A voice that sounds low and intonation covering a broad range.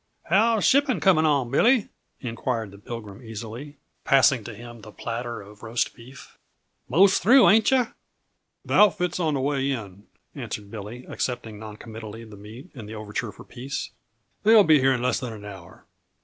Yes: low, 120 Hz; wide, 6.3 semitones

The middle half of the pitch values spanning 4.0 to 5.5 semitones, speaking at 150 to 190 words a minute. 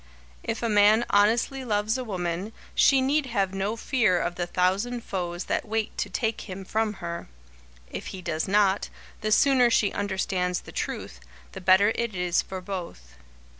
No: average, 3.6 semitones; average, 170 wpm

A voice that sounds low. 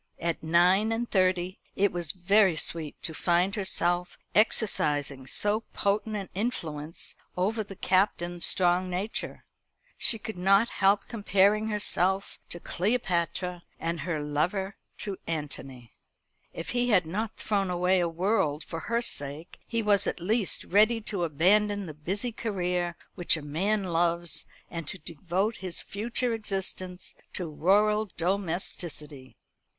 No: medium, 185 Hz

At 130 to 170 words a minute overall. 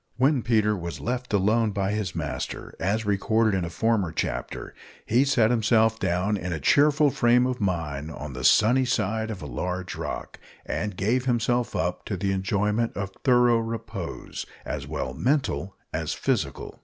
Yes: average, 165 wpm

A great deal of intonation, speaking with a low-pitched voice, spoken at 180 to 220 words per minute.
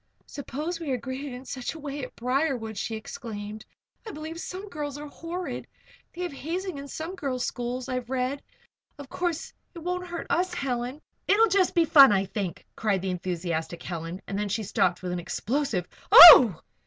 No: wide, 7.3 semitones; very high, 265 Hz; average, 190 wpm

